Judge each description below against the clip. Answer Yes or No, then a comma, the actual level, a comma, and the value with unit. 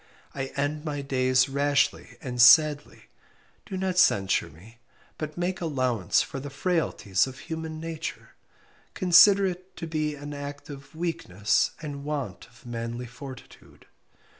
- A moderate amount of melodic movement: Yes, average, 4.3 semitones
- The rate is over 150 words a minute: No, average, 140 wpm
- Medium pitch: Yes, medium, 145 Hz